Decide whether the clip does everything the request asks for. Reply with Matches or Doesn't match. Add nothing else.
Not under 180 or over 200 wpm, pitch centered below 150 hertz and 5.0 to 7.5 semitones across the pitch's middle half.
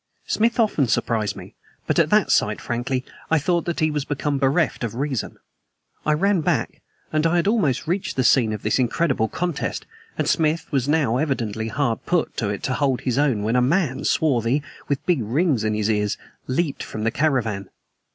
Matches